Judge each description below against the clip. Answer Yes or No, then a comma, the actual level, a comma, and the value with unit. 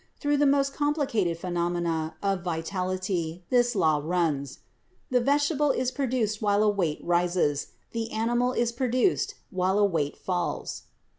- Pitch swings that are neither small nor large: No, wide, 6.5 semitones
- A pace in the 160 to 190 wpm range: No, average, 140 wpm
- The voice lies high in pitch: Yes, high, 200 Hz